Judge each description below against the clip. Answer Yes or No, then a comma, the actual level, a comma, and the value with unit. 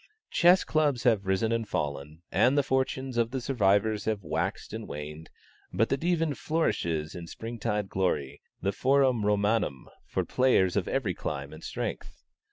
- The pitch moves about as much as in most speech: No, wide, 6.6 semitones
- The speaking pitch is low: Yes, low, 110 Hz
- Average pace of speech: Yes, average, 165 wpm